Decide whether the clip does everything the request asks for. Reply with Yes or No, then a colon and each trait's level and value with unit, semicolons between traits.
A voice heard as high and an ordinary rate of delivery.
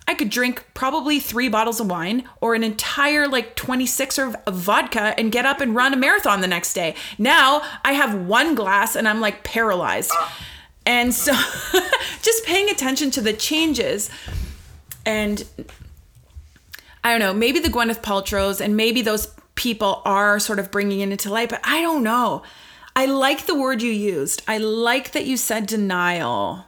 Yes: high, 235 Hz; average, 175 wpm